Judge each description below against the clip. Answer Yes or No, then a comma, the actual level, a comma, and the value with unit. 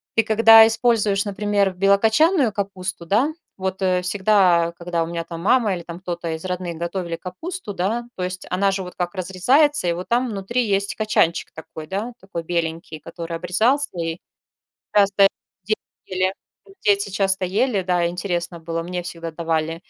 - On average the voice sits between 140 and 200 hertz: Yes, high, 190 Hz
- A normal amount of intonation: Yes, average, 3.5 semitones